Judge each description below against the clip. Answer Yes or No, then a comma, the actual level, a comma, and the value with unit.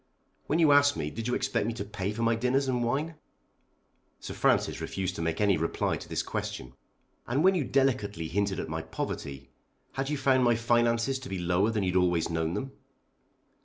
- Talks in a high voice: No, low, 115 Hz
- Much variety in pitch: Yes, wide, 6.9 semitones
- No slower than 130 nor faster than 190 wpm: No, average, 200 wpm